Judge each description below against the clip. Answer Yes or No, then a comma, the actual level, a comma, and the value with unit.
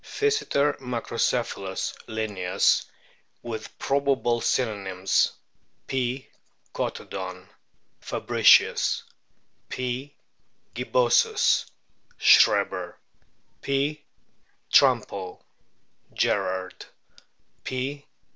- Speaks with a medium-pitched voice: No, low, 125 Hz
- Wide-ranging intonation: Yes, wide, 6.0 semitones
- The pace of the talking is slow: Yes, slow, 50 wpm